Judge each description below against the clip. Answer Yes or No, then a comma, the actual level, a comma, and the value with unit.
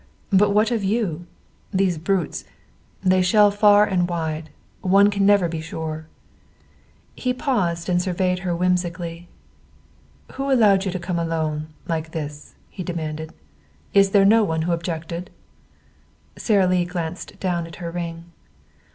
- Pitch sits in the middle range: Yes, medium, 180 Hz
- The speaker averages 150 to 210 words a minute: No, average, 140 wpm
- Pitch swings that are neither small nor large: Yes, average, 3.0 semitones